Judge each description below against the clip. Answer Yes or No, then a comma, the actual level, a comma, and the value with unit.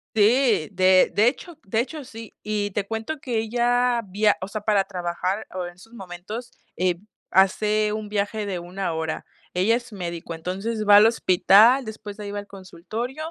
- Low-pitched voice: No, high, 210 Hz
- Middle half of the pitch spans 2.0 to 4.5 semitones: Yes, average, 3.3 semitones